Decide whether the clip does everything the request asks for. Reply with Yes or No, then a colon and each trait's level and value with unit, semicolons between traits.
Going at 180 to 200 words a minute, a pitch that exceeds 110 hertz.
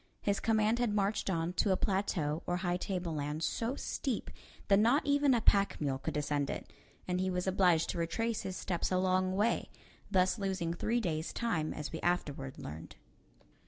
Yes: average, 185 wpm; medium, 185 Hz